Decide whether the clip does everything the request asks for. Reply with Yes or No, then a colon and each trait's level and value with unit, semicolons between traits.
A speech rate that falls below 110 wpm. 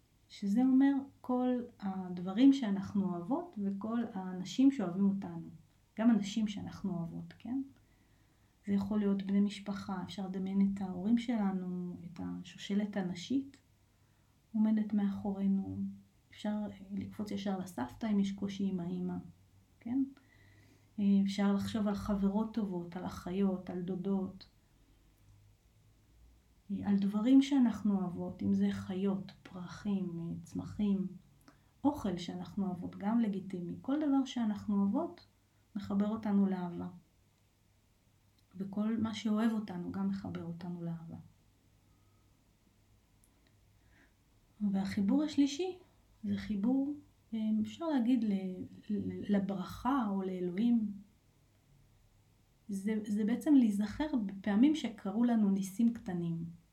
Yes: slow, 100 wpm